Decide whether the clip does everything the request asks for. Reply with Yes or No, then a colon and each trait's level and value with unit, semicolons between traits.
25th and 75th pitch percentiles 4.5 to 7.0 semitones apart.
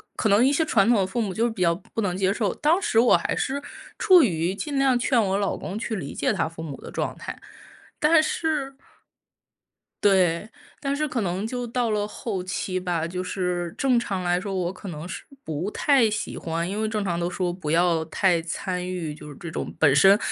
Yes: average, 5.0 semitones